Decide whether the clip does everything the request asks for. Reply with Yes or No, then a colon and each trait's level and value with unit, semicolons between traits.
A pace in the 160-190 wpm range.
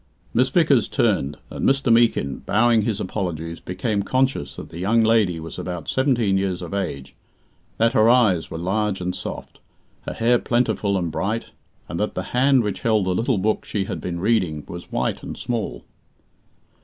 Yes: average, 180 wpm